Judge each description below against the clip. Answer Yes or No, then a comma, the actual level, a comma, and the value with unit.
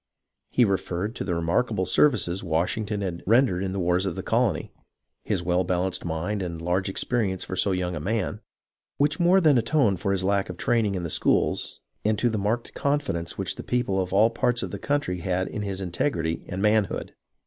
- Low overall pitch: Yes, very low, 95 Hz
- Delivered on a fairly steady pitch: No, average, 4.0 semitones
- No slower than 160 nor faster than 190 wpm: No, fast, 205 wpm